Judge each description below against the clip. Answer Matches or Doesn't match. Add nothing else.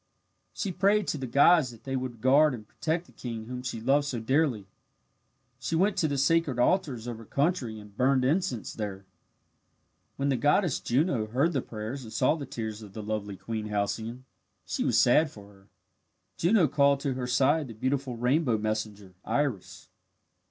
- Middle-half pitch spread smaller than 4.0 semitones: Doesn't match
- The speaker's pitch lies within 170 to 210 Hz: Doesn't match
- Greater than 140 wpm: Matches